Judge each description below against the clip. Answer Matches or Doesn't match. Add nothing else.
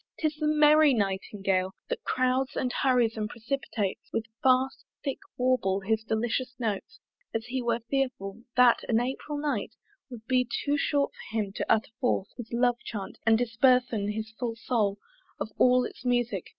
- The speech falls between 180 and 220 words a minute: Doesn't match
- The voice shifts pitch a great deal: Doesn't match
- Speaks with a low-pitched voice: Doesn't match